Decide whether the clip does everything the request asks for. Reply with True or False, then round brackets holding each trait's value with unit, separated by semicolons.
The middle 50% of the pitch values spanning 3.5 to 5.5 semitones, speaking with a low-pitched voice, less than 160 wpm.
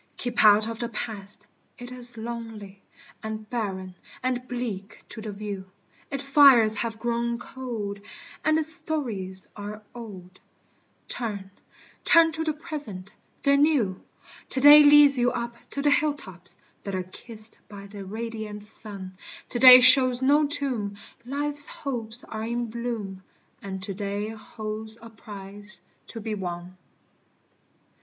False (3.9 semitones; 225 Hz; 140 wpm)